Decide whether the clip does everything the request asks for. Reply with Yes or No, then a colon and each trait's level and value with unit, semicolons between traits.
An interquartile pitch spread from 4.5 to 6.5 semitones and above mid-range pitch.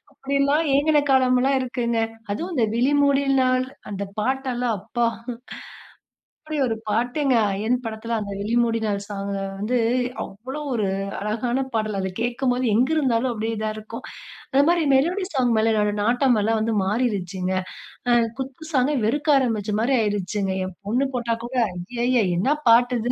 No: average, 3.7 semitones; high, 240 Hz